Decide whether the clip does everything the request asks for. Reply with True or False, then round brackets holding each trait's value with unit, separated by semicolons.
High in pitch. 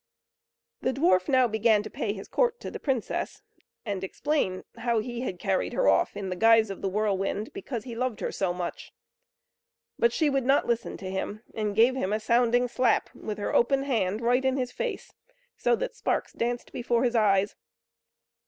True (230 Hz)